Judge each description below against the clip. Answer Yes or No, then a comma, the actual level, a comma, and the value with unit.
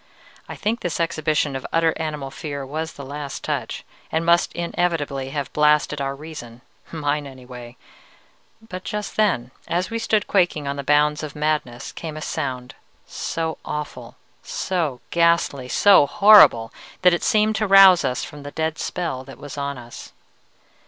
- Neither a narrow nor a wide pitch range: Yes, average, 3.7 semitones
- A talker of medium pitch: Yes, medium, 150 Hz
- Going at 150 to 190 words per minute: Yes, average, 160 wpm